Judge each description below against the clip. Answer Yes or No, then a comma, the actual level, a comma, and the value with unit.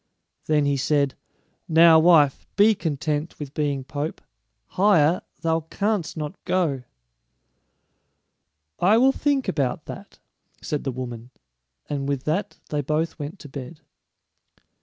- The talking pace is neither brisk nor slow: No, slow, 125 wpm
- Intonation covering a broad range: No, average, 3.2 semitones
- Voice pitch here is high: No, medium, 150 Hz